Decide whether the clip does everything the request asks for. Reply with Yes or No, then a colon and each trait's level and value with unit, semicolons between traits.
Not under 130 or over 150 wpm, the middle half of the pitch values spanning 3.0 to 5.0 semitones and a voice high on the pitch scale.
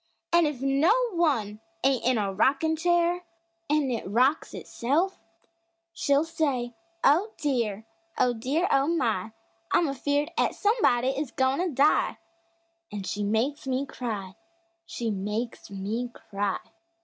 No: slow, 135 wpm; wide, 5.4 semitones; very high, 265 Hz